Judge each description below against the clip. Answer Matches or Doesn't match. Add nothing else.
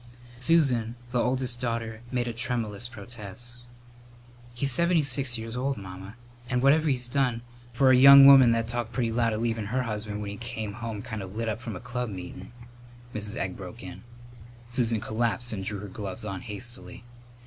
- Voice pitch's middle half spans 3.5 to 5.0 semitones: Doesn't match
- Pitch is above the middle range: Doesn't match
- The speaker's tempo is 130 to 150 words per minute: Doesn't match